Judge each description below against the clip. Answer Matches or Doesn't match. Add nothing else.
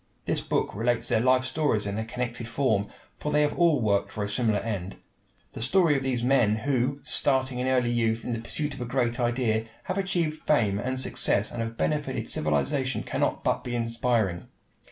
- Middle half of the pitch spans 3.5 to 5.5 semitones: Doesn't match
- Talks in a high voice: Doesn't match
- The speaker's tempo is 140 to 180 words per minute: Doesn't match